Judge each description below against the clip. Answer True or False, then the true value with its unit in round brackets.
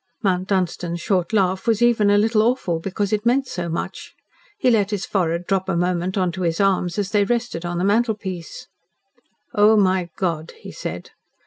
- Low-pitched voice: False (190 Hz)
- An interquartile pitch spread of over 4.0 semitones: False (3.2 semitones)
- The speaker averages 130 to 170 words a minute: False (190 wpm)